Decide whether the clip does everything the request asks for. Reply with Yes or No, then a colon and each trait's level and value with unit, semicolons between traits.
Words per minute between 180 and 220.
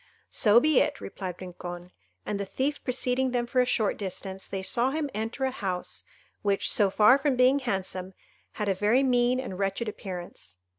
Yes: average, 185 wpm